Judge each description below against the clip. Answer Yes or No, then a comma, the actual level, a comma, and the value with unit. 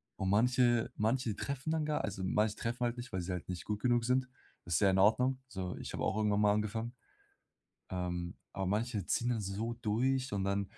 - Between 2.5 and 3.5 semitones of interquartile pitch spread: No, average, 4.0 semitones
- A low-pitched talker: Yes, low, 110 Hz